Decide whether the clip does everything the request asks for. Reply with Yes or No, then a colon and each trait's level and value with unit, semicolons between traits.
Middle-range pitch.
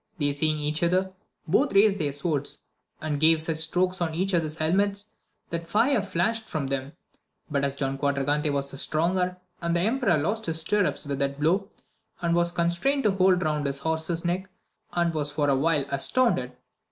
Yes: medium, 165 Hz